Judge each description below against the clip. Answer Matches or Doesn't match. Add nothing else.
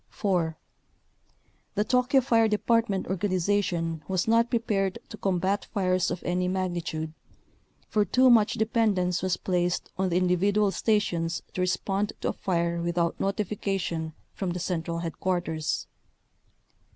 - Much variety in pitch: Doesn't match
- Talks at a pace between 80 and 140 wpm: Matches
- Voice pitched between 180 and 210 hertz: Matches